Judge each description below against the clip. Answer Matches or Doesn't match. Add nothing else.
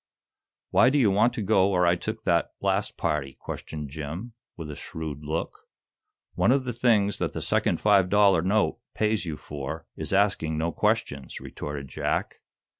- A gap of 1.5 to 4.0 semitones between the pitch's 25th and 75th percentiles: Doesn't match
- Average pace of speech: Matches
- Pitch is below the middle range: Matches